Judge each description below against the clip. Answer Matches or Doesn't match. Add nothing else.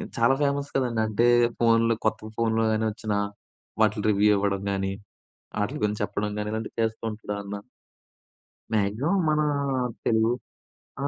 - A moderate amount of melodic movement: Doesn't match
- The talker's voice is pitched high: Doesn't match